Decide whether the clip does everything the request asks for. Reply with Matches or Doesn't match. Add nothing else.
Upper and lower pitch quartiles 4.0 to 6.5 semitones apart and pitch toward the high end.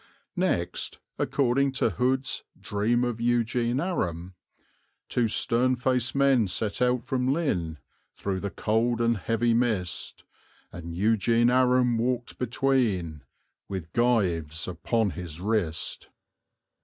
Doesn't match